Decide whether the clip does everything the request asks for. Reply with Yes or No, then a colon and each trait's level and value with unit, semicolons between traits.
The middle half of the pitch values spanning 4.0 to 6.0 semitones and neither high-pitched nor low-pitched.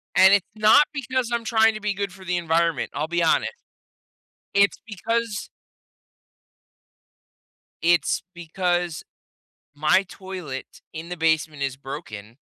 Yes: average, 4.5 semitones; medium, 175 Hz